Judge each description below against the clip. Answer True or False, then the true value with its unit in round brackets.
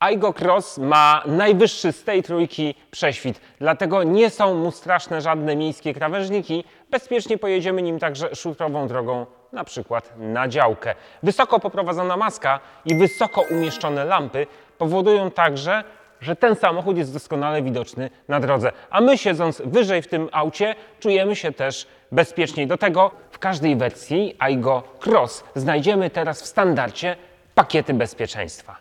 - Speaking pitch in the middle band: True (165 Hz)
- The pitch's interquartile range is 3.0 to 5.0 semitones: False (5.5 semitones)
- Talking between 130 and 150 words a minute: True (140 wpm)